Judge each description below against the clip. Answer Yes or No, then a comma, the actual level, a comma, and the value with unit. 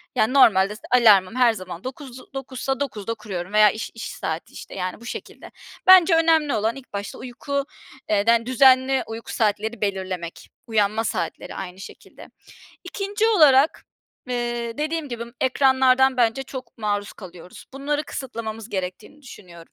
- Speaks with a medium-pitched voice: No, high, 235 Hz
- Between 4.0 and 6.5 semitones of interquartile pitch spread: Yes, average, 4.6 semitones